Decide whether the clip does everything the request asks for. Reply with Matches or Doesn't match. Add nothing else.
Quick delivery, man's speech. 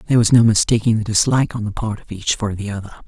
Doesn't match